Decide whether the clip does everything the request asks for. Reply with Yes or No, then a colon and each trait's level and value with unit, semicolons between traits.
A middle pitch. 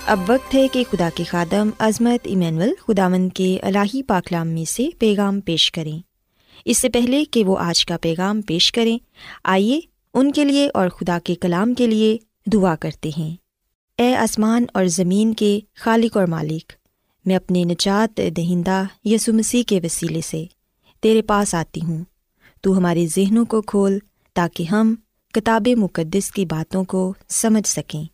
No: high, 195 Hz